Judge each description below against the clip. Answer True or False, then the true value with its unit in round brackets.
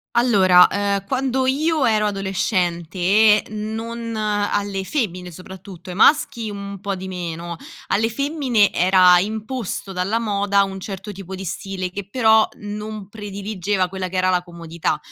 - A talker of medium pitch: False (200 Hz)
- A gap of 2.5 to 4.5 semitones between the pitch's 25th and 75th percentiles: True (2.8 semitones)